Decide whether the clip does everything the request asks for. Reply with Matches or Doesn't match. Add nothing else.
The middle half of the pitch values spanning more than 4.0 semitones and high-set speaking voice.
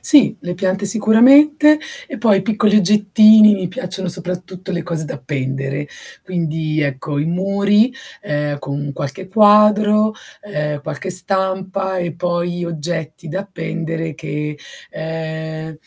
Doesn't match